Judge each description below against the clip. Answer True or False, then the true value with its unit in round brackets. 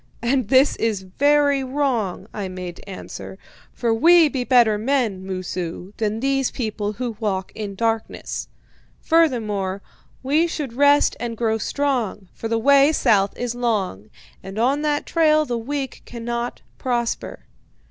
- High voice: True (235 Hz)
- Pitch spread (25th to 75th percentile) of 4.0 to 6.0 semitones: True (5.0 semitones)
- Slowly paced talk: False (145 wpm)